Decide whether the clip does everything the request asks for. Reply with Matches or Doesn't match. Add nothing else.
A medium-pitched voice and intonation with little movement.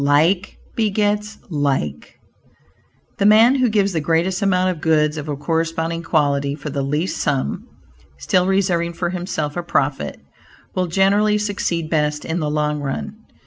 Doesn't match